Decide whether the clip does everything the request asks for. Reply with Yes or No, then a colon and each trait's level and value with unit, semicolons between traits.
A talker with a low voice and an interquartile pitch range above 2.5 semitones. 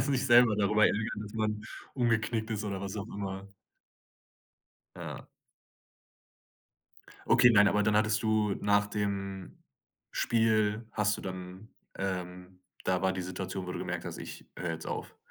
No: low, 105 Hz; narrow, 2.2 semitones